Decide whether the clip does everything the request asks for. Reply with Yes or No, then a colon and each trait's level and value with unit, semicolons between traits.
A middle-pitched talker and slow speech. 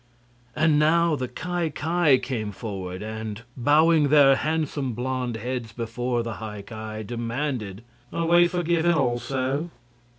No: low, 130 Hz; slow, 130 wpm